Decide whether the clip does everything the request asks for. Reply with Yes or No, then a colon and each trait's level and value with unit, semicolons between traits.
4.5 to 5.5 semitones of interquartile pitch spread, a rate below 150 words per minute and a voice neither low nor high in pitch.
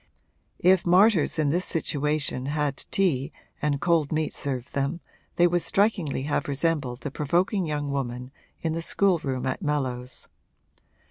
No: average, 3.8 semitones; average, 140 wpm; medium, 150 Hz